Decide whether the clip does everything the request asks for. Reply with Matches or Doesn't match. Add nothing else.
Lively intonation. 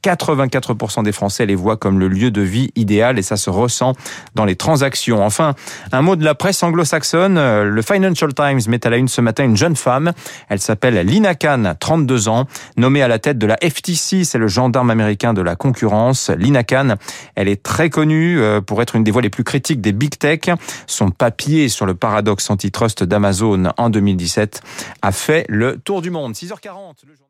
Matches